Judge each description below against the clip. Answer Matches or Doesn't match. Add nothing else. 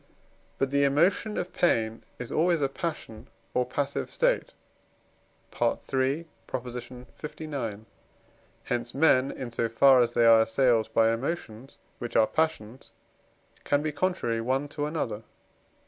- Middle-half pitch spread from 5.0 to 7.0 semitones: Doesn't match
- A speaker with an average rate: Doesn't match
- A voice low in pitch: Matches